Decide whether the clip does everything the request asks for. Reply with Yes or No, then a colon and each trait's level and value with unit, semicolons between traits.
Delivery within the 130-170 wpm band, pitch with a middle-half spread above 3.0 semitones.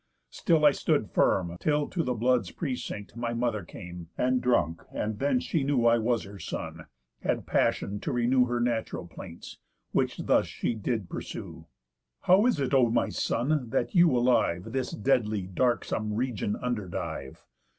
Yes: average, 160 wpm; average, 3.5 semitones